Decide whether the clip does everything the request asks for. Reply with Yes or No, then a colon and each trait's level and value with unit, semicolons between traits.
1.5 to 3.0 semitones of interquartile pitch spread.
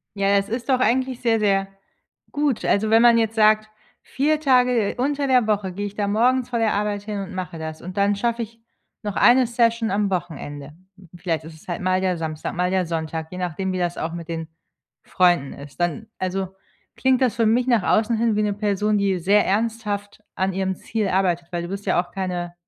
No: average, 4.1 semitones